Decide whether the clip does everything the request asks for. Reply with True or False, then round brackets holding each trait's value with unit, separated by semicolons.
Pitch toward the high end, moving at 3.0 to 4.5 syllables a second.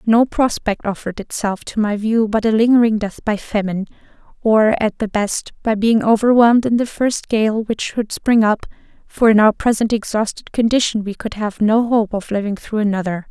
False (220 Hz; 5.1 syllables/s)